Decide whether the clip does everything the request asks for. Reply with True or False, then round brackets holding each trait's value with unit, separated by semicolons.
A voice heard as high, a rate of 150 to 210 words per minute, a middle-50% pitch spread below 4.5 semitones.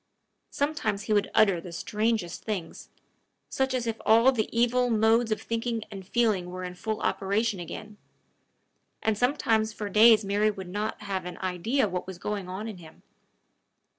True (215 Hz; 170 wpm; 3.2 semitones)